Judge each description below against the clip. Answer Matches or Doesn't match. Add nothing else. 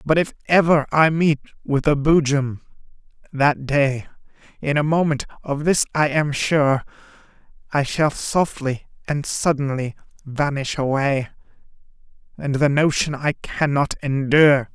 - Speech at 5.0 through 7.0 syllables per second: Doesn't match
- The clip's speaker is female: Doesn't match